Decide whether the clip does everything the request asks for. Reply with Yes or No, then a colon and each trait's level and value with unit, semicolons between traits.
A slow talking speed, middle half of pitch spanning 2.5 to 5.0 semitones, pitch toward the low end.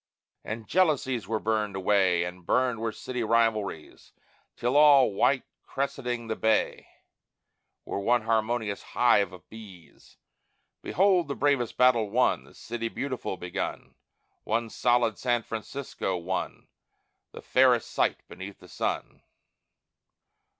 Yes: slow, 120 wpm; average, 3.7 semitones; low, 115 Hz